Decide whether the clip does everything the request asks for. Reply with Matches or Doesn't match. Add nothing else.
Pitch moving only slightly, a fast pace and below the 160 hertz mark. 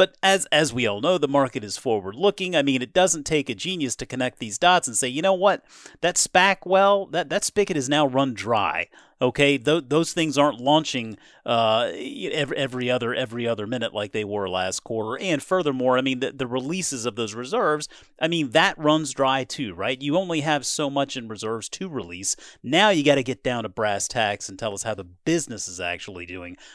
Doesn't match